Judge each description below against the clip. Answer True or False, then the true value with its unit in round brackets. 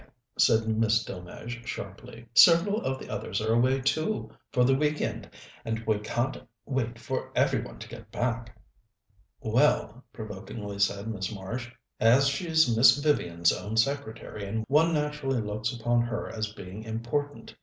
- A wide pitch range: False (3.6 semitones)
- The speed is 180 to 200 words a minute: False (150 wpm)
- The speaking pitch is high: False (115 Hz)